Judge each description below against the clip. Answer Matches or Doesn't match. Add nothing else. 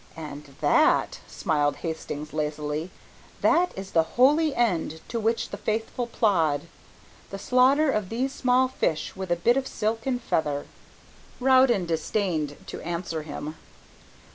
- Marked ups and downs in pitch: Matches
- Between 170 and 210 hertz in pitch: Matches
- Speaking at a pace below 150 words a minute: Matches